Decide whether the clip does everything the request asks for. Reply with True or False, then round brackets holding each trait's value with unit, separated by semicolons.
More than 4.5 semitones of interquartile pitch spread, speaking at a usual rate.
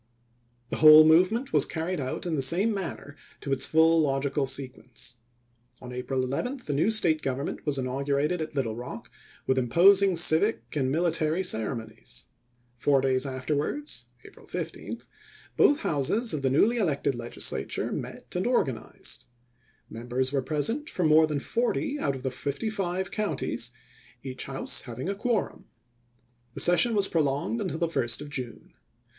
True (5.3 semitones; 160 wpm)